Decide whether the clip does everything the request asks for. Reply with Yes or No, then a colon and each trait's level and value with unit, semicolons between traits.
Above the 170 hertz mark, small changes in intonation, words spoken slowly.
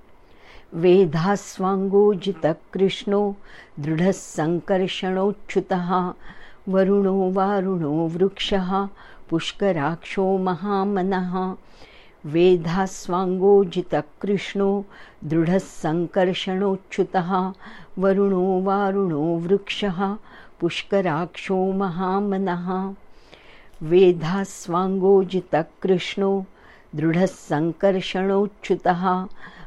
Yes: high, 190 Hz; narrow, 1.7 semitones; slow, 30 wpm